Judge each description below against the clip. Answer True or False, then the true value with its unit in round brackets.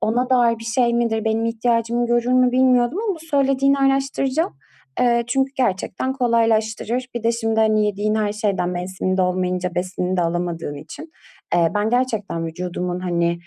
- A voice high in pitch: True (225 Hz)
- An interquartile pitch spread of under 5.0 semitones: False (5.3 semitones)